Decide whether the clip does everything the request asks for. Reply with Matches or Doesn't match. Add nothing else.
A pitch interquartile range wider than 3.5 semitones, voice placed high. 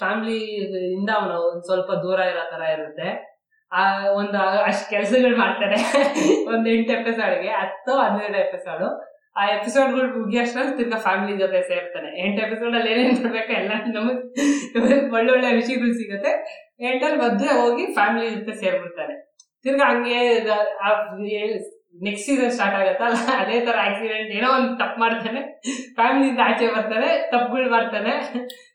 Matches